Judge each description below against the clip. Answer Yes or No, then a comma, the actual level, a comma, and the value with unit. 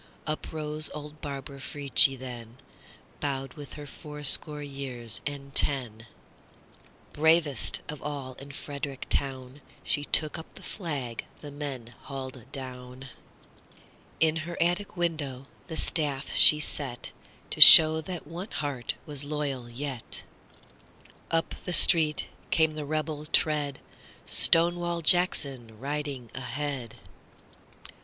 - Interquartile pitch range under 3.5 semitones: Yes, average, 2.7 semitones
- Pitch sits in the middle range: Yes, medium, 145 Hz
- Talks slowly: Yes, slow, 105 wpm